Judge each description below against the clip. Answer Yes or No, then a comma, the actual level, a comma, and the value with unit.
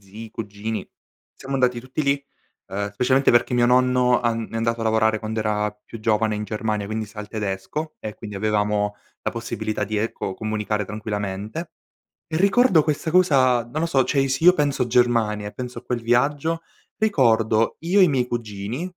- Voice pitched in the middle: No, low, 115 Hz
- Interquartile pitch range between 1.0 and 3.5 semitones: No, average, 4.0 semitones